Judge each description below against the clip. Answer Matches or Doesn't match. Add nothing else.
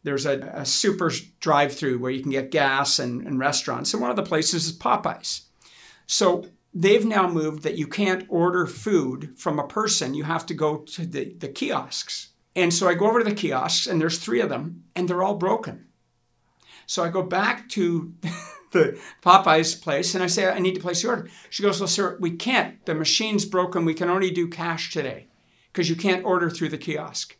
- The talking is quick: Matches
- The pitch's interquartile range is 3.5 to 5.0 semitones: Doesn't match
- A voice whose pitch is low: Doesn't match